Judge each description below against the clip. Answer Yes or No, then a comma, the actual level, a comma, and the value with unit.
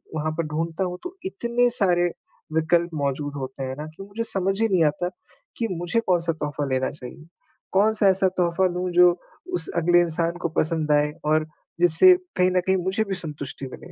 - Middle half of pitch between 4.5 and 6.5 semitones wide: No, average, 3.4 semitones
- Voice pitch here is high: No, medium, 175 Hz